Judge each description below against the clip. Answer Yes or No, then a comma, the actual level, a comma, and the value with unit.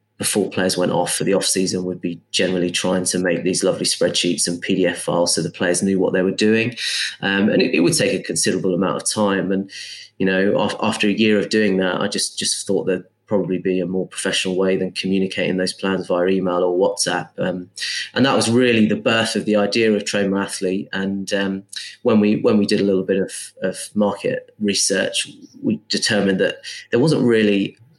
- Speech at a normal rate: No, fast, 210 wpm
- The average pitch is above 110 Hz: No, very low, 95 Hz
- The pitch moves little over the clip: Yes, narrow, 2.1 semitones